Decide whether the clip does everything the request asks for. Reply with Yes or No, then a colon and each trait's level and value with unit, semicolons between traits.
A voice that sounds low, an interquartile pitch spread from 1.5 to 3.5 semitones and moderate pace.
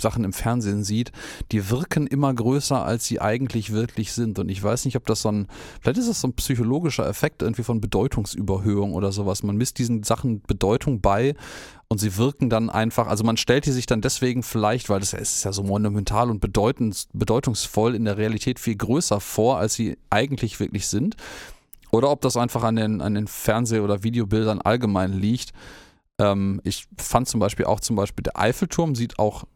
No: low, 115 Hz; average, 3.0 semitones; fast, 195 wpm